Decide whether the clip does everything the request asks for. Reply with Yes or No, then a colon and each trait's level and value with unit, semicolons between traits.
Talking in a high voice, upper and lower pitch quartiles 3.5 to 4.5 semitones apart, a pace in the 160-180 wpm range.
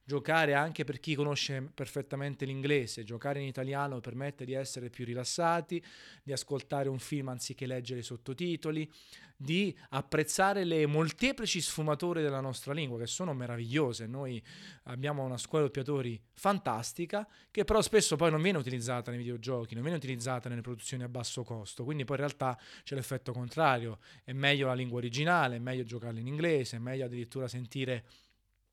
No: low, 135 Hz; average, 3.8 semitones; average, 165 wpm